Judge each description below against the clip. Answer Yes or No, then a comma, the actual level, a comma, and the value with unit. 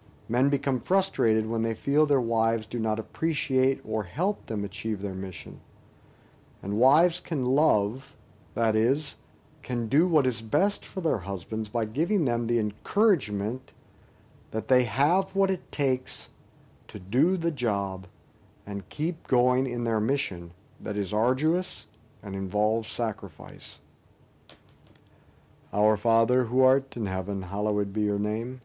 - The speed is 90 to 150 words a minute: Yes, average, 140 wpm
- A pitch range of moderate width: Yes, average, 4.6 semitones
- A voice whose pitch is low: Yes, low, 115 Hz